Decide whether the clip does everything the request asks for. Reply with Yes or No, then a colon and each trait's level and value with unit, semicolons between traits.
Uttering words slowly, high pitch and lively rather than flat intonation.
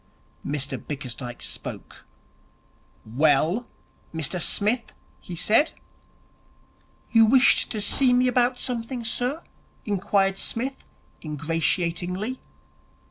Yes: slow, 85 wpm; high, 200 Hz; wide, 7.5 semitones